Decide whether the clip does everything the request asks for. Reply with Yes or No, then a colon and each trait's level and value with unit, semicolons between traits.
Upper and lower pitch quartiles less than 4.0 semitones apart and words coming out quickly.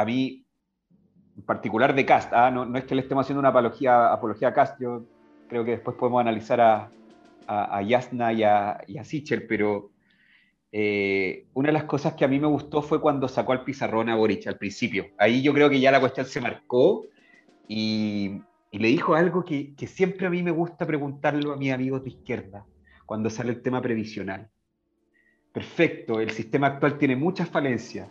No: average, 4.9 semitones; fast, 195 wpm